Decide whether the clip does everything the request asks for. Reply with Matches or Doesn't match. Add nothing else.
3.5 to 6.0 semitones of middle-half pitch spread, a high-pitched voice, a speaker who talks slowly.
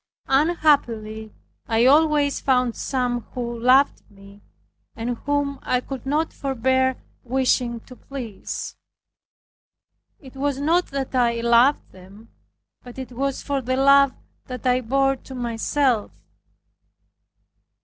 Doesn't match